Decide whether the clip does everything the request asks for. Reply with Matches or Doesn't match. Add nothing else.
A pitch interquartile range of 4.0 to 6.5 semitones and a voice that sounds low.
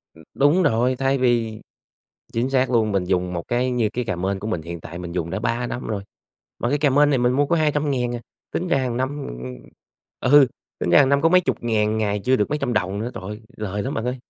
Matches